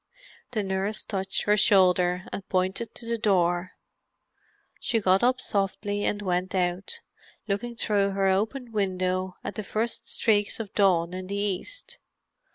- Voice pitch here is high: Yes, high, 200 Hz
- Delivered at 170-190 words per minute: No, average, 150 wpm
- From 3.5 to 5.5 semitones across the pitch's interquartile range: No, narrow, 2.6 semitones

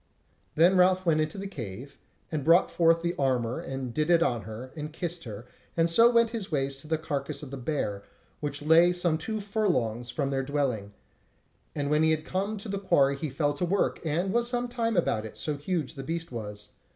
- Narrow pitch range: No, average, 4.9 semitones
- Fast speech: Yes, fast, 215 wpm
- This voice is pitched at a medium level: Yes, medium, 155 Hz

